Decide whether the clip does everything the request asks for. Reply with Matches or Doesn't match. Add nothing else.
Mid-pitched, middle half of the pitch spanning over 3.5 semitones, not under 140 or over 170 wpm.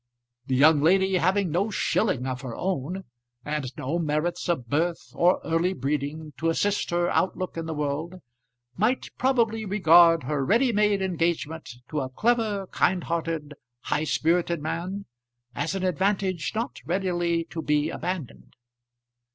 Matches